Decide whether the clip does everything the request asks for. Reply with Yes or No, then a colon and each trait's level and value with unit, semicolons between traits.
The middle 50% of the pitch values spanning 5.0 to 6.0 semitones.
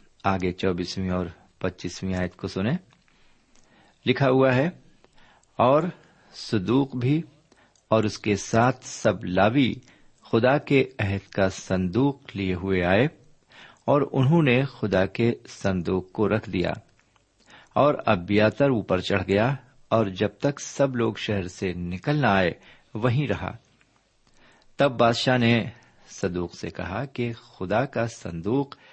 Yes: wide, 5.4 semitones